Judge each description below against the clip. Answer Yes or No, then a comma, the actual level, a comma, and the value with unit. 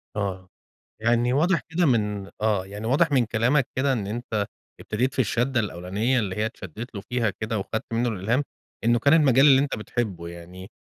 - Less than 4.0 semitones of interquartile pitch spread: No, average, 4.3 semitones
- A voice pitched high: No, low, 115 Hz